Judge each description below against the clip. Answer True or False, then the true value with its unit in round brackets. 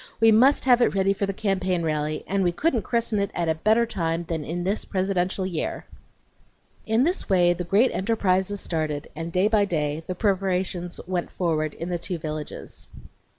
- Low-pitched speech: False (185 Hz)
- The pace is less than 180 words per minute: False (195 wpm)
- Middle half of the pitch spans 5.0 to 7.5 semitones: False (3.3 semitones)